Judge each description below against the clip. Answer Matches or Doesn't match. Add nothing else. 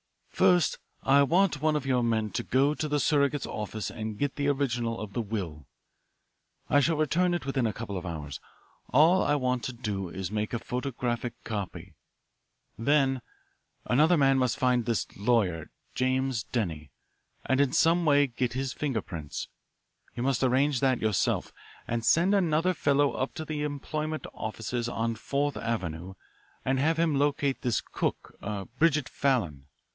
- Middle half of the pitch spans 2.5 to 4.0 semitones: Doesn't match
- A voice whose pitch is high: Doesn't match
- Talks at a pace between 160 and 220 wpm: Matches